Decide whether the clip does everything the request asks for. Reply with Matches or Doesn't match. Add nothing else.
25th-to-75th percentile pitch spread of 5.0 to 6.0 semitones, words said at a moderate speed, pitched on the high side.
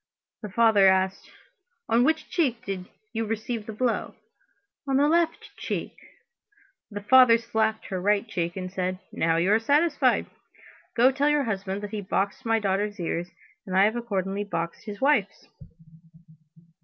Doesn't match